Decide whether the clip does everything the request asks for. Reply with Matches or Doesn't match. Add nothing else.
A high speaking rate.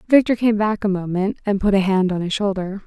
Matches